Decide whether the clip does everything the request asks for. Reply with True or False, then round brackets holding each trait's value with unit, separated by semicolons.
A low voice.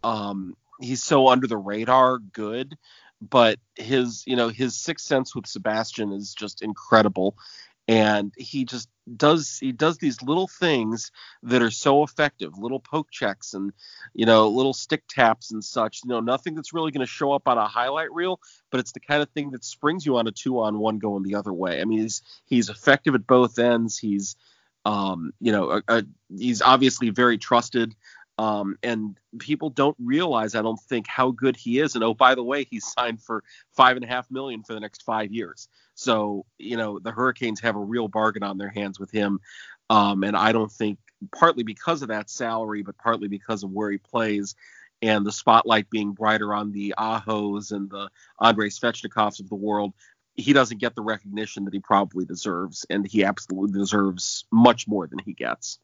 True (115 Hz)